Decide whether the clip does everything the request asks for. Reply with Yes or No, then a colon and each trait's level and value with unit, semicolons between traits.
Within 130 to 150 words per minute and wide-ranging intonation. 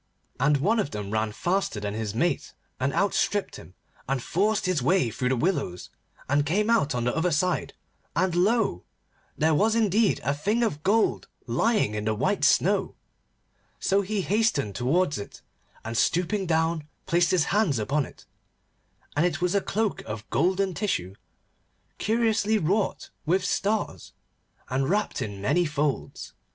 No: average, 160 wpm; wide, 7.6 semitones